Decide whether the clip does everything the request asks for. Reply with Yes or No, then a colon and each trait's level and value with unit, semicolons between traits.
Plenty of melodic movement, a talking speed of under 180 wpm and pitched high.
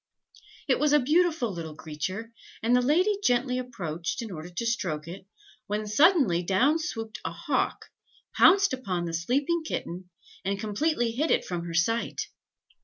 Yes: wide, 8.2 semitones; average, 160 wpm; high, 230 Hz